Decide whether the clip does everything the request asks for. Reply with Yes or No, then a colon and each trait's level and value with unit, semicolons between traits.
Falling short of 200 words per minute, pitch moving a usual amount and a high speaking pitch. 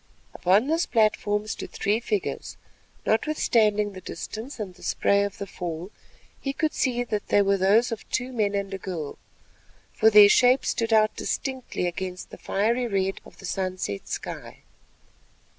Yes: average, 160 wpm; average, 3.3 semitones; high, 210 Hz